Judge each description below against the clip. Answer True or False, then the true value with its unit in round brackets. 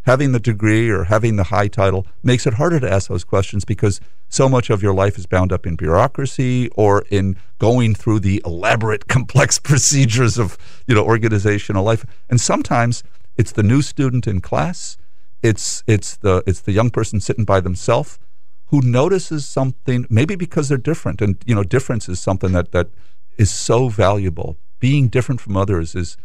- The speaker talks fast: False (185 wpm)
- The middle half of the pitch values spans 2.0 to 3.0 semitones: False (4.3 semitones)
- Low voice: True (110 Hz)